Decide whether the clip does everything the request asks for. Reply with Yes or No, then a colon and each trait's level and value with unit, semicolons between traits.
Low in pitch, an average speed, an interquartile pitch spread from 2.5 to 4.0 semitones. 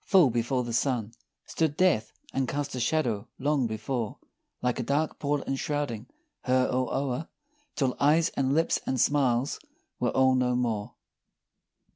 Yes: low, 130 Hz; average, 150 wpm; average, 3.1 semitones